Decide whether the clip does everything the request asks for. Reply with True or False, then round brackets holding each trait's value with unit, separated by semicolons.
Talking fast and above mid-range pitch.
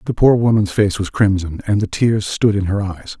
False (245 wpm; 100 Hz)